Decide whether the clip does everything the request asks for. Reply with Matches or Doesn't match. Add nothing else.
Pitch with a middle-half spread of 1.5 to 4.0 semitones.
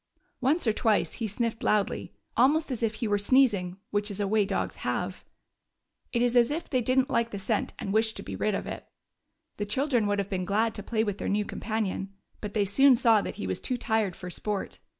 Matches